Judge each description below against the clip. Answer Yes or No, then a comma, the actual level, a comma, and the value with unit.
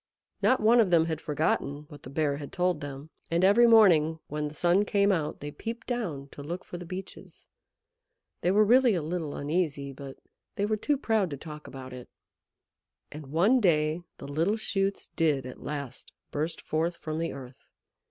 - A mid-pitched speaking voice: Yes, medium, 160 Hz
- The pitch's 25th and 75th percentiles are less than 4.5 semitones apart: No, average, 5.2 semitones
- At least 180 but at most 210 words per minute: Yes, average, 190 wpm